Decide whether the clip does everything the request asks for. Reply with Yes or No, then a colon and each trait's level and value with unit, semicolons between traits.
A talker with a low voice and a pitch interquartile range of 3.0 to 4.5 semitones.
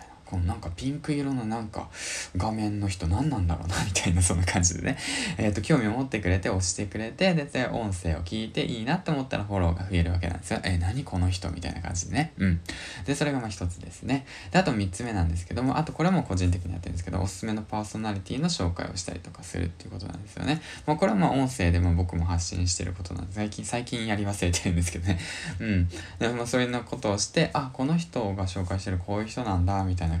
No: very low, 95 Hz; average, 5.2 semitones